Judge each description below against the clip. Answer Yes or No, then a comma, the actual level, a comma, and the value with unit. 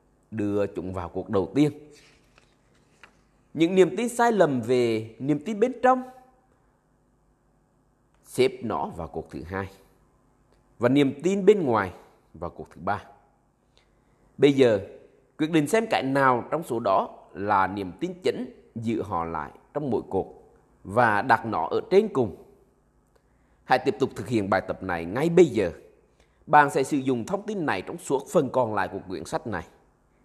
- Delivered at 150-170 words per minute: Yes, slow, 165 wpm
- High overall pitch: No, medium, 150 Hz